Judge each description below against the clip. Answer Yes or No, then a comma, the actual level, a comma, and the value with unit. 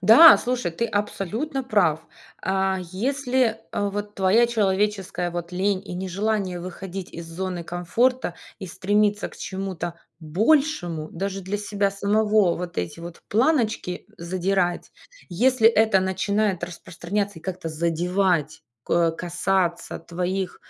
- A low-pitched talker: No, high, 190 Hz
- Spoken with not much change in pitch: No, average, 3.2 semitones